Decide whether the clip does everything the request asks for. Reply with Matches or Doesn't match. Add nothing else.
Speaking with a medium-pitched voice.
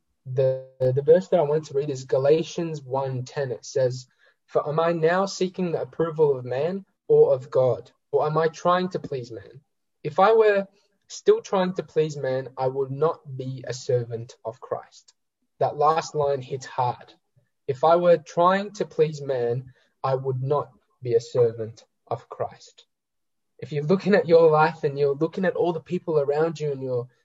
Matches